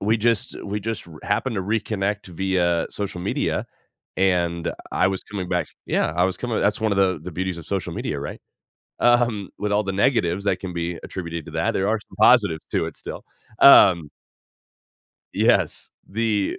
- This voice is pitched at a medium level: No, very low, 95 Hz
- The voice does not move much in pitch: No, average, 3.1 semitones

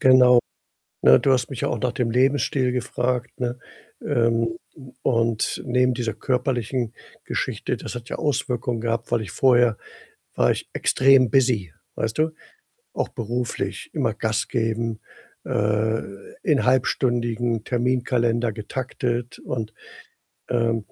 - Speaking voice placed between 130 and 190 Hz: No, low, 120 Hz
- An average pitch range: No, narrow, 1.8 semitones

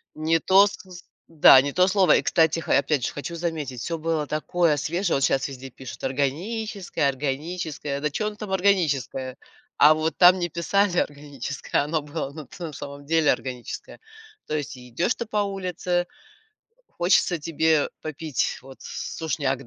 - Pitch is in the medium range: Yes, medium, 155 Hz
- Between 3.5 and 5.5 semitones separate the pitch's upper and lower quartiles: Yes, average, 3.9 semitones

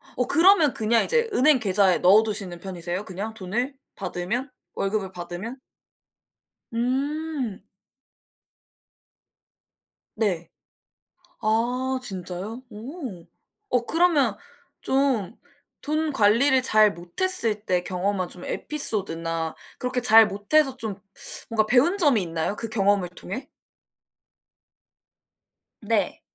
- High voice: Yes, high, 220 Hz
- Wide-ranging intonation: Yes, wide, 5.8 semitones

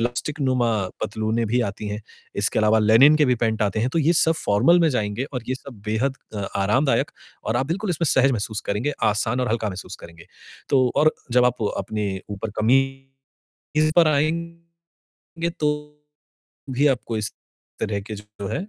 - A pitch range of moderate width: Yes, average, 5.0 semitones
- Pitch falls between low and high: No, low, 125 Hz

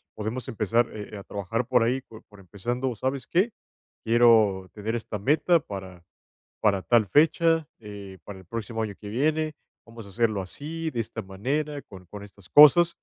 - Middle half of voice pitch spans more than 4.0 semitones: Yes, average, 5.0 semitones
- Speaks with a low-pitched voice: Yes, low, 115 Hz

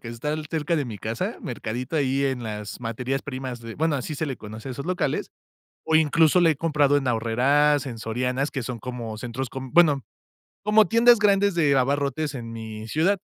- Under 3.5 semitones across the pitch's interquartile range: No, average, 4.5 semitones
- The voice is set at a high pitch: No, low, 135 Hz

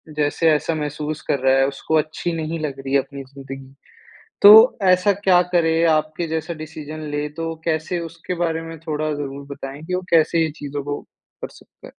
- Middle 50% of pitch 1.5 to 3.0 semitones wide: Yes, narrow, 2.4 semitones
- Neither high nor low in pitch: Yes, medium, 155 Hz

